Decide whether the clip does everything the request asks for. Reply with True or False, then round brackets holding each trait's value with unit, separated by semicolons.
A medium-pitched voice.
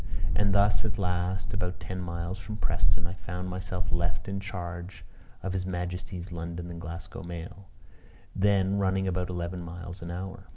False (90 Hz)